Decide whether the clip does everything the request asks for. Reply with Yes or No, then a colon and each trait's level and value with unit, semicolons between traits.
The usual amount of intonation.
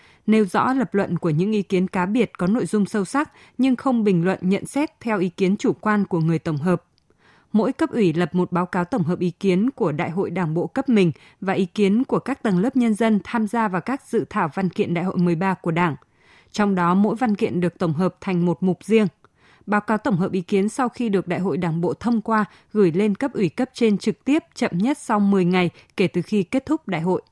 Yes: average, 3.8 semitones